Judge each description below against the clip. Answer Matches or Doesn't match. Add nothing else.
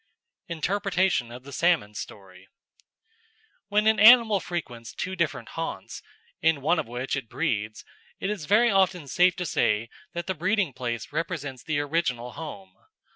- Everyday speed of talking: Matches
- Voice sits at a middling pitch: Matches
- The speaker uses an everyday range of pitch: Doesn't match